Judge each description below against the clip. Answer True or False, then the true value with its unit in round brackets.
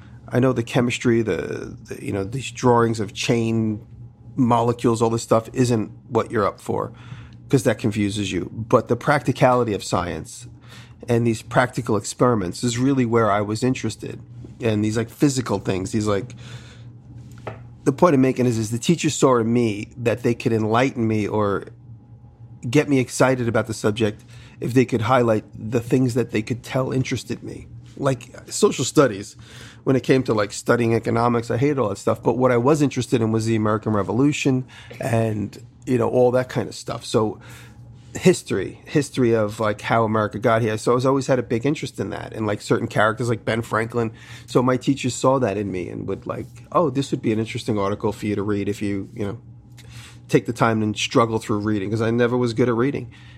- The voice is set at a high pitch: False (120 Hz)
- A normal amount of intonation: False (2.3 semitones)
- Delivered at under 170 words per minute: False (200 wpm)